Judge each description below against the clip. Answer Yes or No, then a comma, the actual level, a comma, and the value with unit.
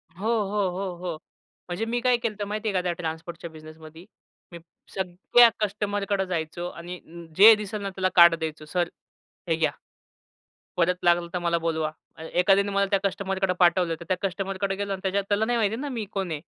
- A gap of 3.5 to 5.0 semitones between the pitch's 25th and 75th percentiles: No, average, 2.9 semitones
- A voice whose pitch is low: No, high, 190 Hz